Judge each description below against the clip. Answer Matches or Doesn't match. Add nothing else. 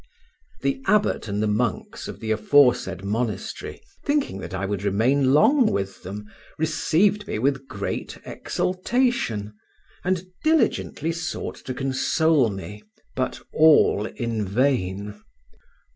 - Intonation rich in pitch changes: Matches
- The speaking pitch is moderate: Doesn't match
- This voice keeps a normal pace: Doesn't match